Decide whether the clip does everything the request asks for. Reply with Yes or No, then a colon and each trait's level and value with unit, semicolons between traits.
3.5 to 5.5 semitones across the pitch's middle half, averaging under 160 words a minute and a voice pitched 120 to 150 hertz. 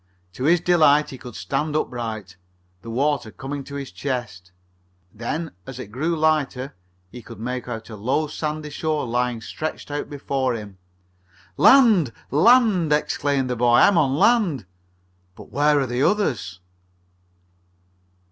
Yes: average, 4.2 semitones; average, 145 wpm; medium, 140 Hz